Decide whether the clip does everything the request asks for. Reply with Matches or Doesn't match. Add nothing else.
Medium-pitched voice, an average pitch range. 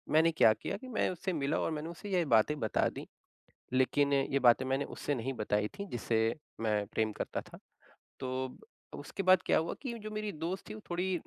Doesn't match